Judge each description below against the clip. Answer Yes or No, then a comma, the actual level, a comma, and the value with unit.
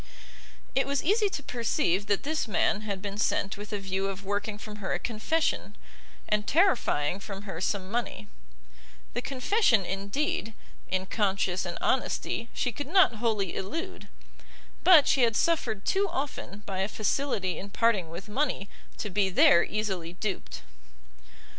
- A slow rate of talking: No, average, 155 wpm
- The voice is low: No, high, 210 Hz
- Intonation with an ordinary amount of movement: Yes, average, 4.8 semitones